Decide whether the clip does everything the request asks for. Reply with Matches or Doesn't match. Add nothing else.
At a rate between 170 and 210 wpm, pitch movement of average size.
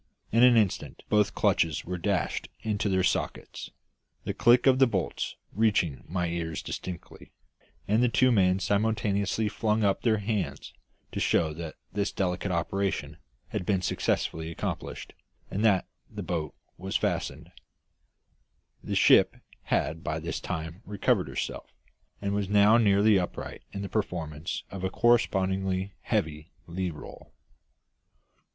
Doesn't match